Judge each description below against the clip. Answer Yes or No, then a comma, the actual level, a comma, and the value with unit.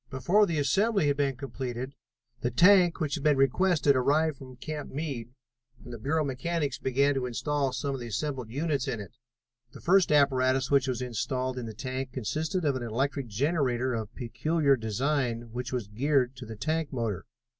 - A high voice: No, low, 135 Hz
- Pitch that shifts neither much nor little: Yes, average, 3.3 semitones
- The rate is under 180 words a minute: No, average, 185 wpm